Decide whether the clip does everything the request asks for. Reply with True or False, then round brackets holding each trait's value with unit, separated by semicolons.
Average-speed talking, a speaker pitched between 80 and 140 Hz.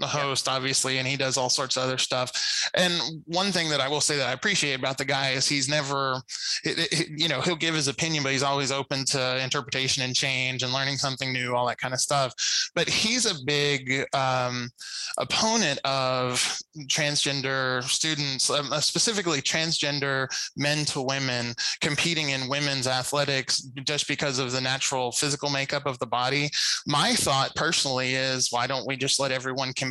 True (185 wpm; 135 Hz)